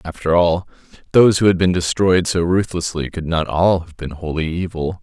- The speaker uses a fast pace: No, average, 190 wpm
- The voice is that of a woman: No, male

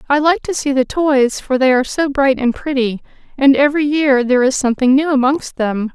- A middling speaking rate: No, fast, 220 wpm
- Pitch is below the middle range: No, very high, 270 Hz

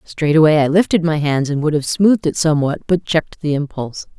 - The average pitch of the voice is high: No, medium, 155 Hz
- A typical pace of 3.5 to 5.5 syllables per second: No, 5.7 syllables/s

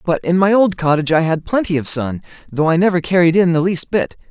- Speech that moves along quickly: Yes, fast, 250 wpm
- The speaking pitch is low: No, medium, 170 Hz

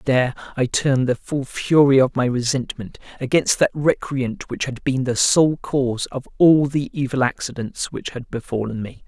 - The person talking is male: Yes, male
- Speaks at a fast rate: No, average, 180 wpm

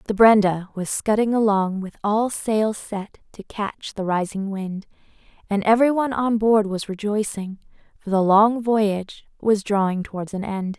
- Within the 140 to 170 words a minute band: Yes, average, 160 wpm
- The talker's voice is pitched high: Yes, high, 205 Hz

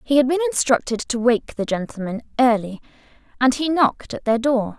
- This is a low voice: No, very high, 250 Hz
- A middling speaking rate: Yes, average, 190 wpm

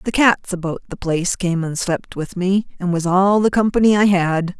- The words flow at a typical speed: No, fast, 220 wpm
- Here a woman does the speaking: Yes, female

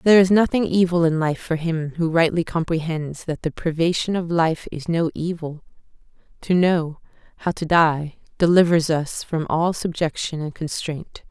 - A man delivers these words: No, female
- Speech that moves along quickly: No, average, 165 wpm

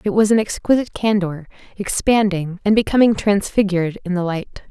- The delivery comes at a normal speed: Yes, average, 155 wpm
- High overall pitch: Yes, high, 200 Hz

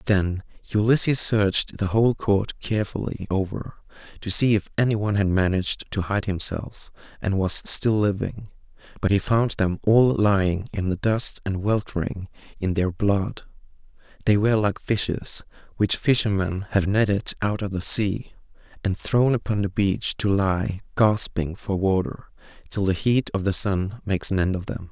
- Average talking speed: Yes, average, 165 wpm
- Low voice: Yes, low, 100 Hz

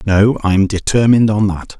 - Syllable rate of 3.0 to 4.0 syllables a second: No, 4.9 syllables/s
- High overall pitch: No, low, 105 Hz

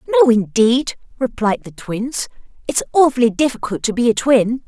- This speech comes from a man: No, female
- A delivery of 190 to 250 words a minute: No, average, 155 wpm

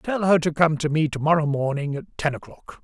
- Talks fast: Yes, fast, 255 wpm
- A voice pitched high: No, medium, 155 Hz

